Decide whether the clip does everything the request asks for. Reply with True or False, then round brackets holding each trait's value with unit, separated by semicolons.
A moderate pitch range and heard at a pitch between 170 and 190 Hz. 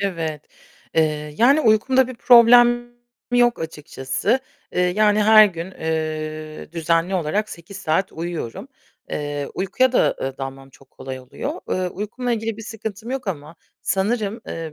False (6.3 semitones; 185 Hz)